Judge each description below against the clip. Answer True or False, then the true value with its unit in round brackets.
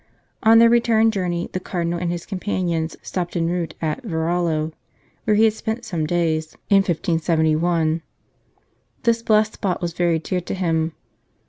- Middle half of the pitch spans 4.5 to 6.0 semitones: False (4.1 semitones)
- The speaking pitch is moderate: True (175 Hz)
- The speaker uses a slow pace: False (155 wpm)